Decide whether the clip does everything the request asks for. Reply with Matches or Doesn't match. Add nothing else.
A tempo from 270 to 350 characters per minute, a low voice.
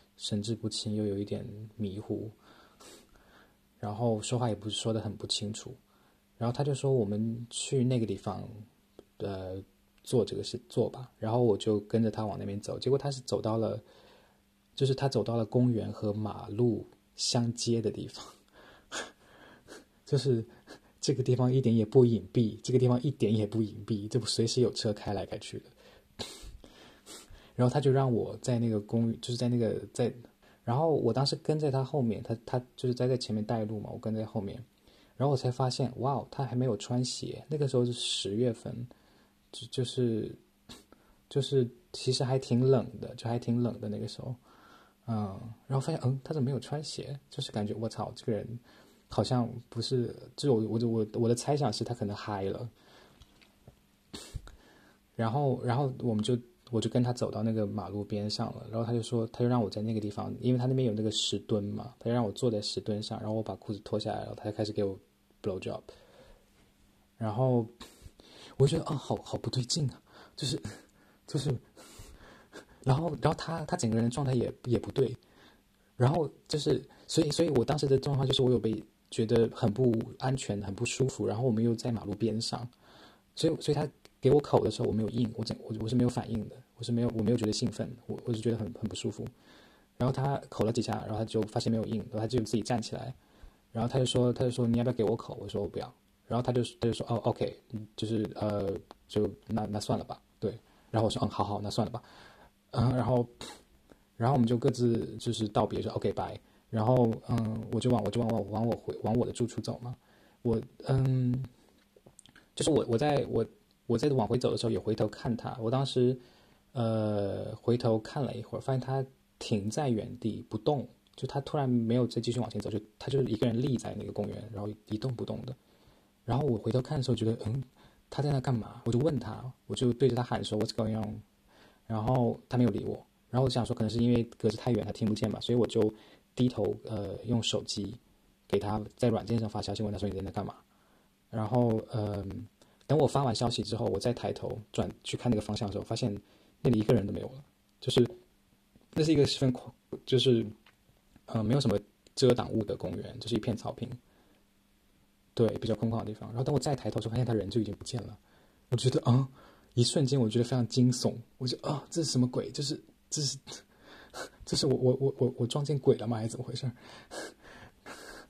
Matches